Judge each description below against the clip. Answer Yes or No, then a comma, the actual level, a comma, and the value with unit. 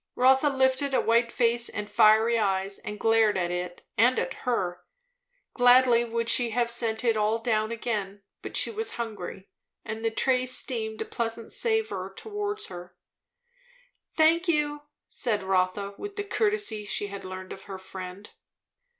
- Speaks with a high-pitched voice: Yes, high, 230 Hz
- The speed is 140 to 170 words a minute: Yes, average, 160 wpm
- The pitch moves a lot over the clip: No, average, 4.1 semitones